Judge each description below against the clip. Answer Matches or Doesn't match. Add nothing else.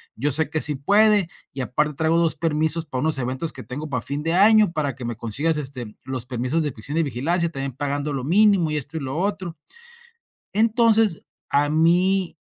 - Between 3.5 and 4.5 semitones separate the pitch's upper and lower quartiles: Matches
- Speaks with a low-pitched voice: Doesn't match